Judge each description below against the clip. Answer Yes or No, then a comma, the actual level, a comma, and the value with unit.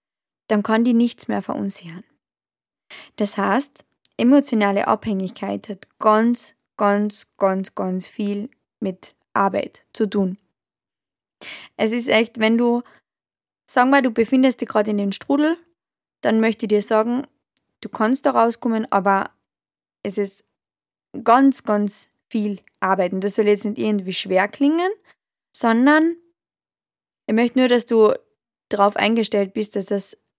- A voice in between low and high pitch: No, high, 215 Hz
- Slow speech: No, average, 140 wpm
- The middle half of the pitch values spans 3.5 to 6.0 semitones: No, average, 3.1 semitones